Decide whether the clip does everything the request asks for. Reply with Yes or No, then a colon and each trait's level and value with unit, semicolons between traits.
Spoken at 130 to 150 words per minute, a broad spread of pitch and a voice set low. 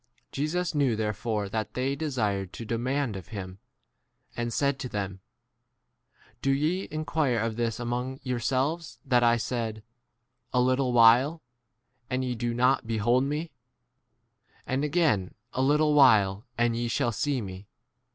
No: average, 140 wpm; average, 3.8 semitones; low, 125 Hz